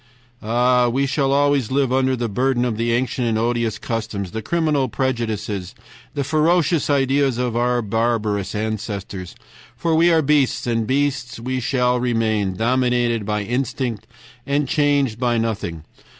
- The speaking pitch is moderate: No, low, 120 Hz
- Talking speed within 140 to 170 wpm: Yes, average, 150 wpm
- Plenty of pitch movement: No, average, 3.3 semitones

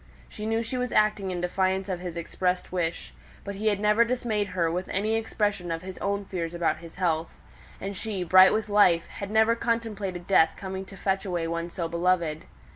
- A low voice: No, high, 190 Hz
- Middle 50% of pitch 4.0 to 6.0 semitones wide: No, average, 3.3 semitones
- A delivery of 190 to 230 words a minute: Yes, average, 200 wpm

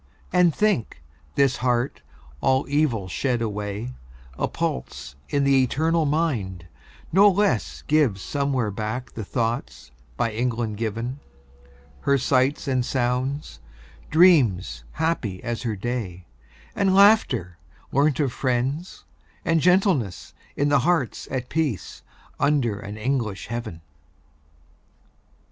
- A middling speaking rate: No, slow, 115 wpm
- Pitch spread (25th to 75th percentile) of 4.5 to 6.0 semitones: Yes, average, 5.2 semitones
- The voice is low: Yes, low, 125 Hz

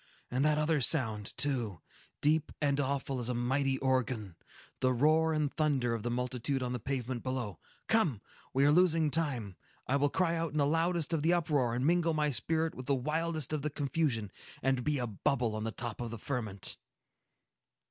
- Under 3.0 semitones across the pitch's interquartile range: No, average, 4.0 semitones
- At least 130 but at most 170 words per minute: No, average, 190 wpm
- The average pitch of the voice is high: No, low, 135 Hz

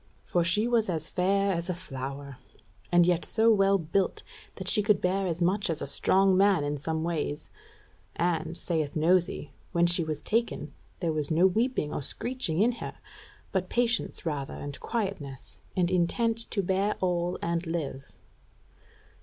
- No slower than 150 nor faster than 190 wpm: Yes, average, 165 wpm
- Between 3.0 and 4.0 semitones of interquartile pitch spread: Yes, average, 3.7 semitones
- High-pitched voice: No, medium, 175 Hz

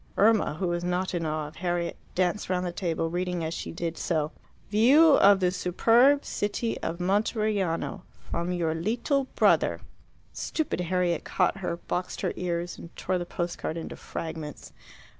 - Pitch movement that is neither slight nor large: Yes, average, 3.1 semitones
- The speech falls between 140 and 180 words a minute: Yes, average, 165 wpm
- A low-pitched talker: No, medium, 180 Hz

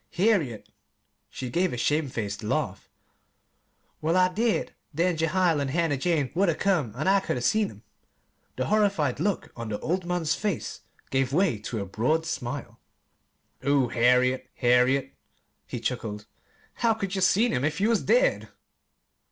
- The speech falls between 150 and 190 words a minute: Yes, average, 160 wpm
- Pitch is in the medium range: Yes, medium, 155 Hz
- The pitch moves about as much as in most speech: No, wide, 6.8 semitones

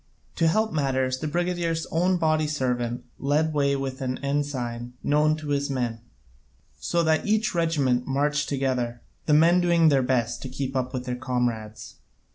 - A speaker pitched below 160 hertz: Yes, medium, 140 Hz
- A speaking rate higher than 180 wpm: No, average, 170 wpm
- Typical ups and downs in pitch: Yes, average, 3.9 semitones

